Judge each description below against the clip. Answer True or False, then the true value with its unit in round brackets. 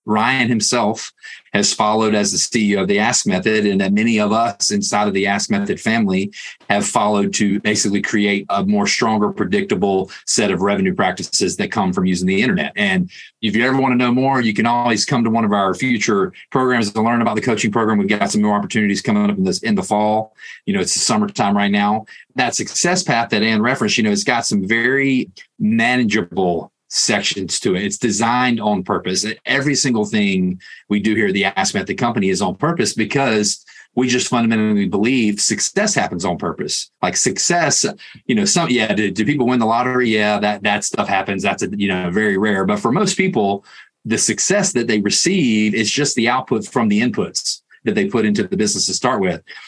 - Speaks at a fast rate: True (215 wpm)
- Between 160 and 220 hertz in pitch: False (115 Hz)